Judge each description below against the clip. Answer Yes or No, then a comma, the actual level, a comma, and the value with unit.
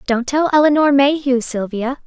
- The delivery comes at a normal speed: Yes, average, 145 wpm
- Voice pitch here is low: No, very high, 270 Hz